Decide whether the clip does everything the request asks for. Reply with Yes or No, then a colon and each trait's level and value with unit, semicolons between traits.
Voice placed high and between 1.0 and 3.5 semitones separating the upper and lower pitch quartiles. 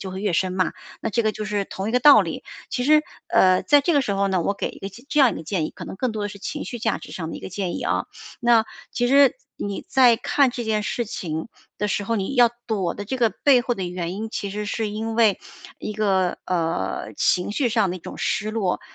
No: high, 210 Hz; average, 3.9 semitones